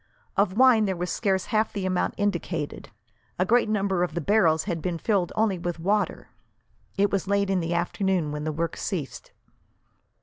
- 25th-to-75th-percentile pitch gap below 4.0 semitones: Yes, average, 3.1 semitones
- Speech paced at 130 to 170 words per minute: No, average, 180 wpm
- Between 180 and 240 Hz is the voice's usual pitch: Yes, medium, 185 Hz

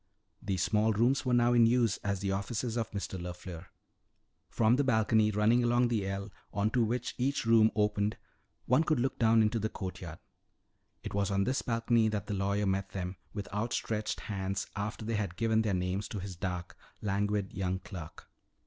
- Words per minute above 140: Yes, average, 185 wpm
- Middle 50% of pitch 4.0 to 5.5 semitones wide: No, average, 2.8 semitones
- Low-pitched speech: Yes, low, 105 Hz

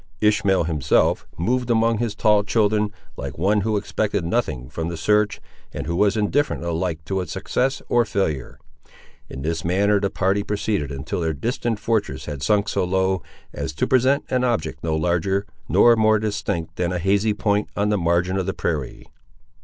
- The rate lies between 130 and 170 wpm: No, average, 180 wpm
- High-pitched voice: No, low, 100 Hz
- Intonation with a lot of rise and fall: No, average, 4.0 semitones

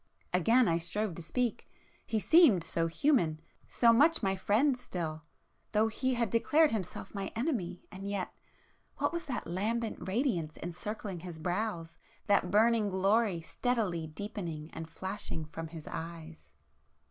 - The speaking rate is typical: No, slow, 130 wpm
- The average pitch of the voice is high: Yes, high, 195 Hz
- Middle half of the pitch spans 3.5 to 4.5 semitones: No, wide, 5.5 semitones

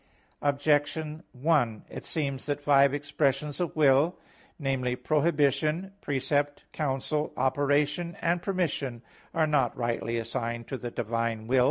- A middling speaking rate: No, slow, 125 wpm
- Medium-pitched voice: Yes, medium, 145 Hz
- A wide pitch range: No, average, 3.1 semitones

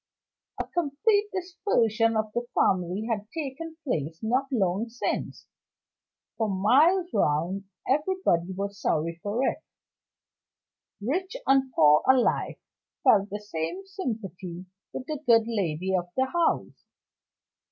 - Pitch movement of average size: No, wide, 7.6 semitones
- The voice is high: Yes, high, 225 Hz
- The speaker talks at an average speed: No, slow, 120 wpm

